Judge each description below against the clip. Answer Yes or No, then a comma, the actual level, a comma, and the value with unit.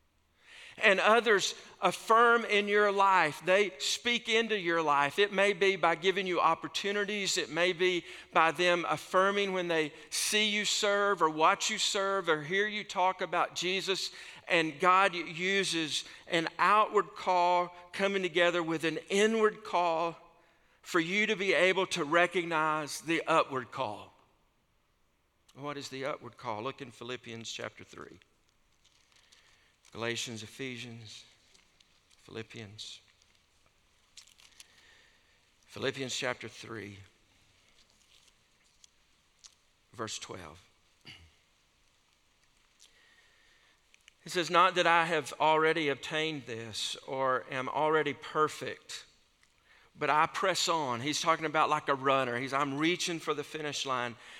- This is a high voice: No, medium, 160 Hz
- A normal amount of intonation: No, wide, 7.1 semitones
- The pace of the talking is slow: Yes, slow, 120 wpm